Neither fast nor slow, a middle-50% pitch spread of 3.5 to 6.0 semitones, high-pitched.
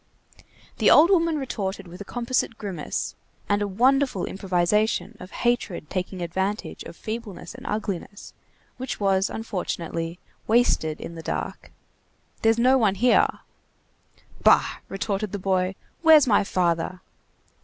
No: slow, 130 wpm; average, 4.5 semitones; high, 205 Hz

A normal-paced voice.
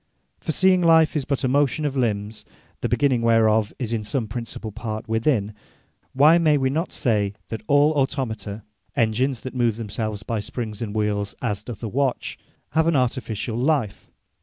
Yes: average, 175 wpm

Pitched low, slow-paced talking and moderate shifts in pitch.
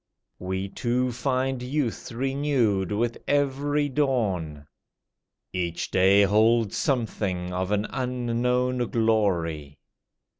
Yes: low, 115 Hz; slow, 90 wpm; average, 5.0 semitones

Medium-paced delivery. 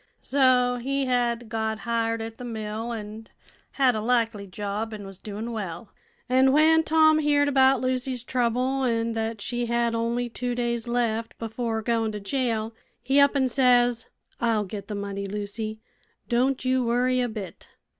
Yes: average, 165 wpm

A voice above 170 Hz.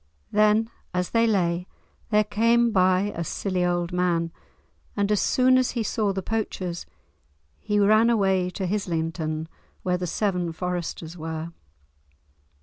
Yes: medium, 185 Hz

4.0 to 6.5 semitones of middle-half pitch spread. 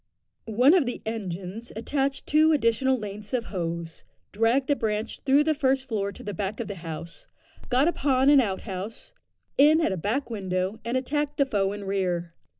Yes: wide, 5.6 semitones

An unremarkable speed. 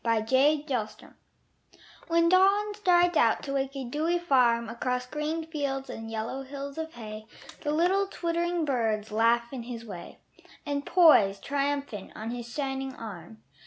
Yes: average, 150 wpm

